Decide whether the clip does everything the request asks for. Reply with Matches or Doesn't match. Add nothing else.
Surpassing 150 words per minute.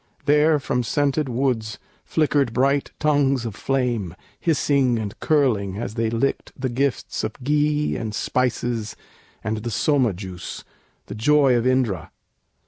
Doesn't match